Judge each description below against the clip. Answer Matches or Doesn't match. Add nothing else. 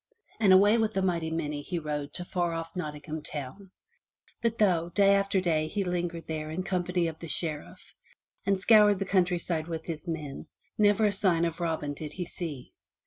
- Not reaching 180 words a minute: Doesn't match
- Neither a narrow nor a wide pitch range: Matches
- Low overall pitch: Doesn't match